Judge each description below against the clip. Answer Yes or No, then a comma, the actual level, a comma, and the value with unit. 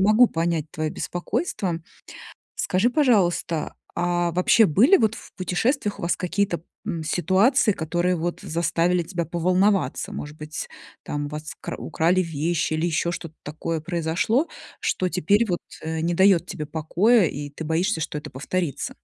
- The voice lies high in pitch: No, medium, 175 Hz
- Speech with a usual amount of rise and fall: Yes, average, 3.2 semitones